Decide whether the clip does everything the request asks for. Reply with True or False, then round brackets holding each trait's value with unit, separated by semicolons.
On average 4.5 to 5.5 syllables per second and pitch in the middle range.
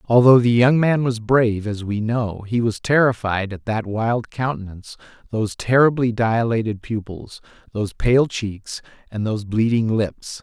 False (4.6 syllables/s; 115 Hz)